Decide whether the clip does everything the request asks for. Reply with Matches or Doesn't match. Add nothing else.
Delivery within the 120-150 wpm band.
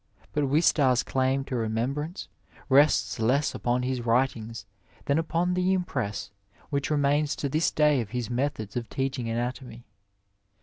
Matches